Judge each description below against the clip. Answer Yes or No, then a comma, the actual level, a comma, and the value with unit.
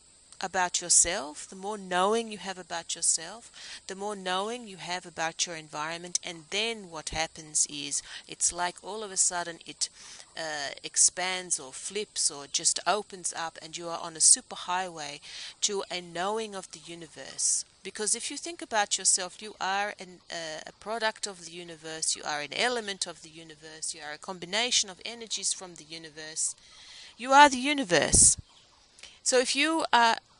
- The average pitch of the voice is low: No, medium, 180 Hz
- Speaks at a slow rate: No, average, 175 wpm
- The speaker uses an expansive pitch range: No, average, 4.2 semitones